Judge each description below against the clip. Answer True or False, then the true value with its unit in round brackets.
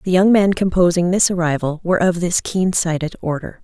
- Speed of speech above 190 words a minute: True (200 wpm)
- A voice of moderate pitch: True (175 Hz)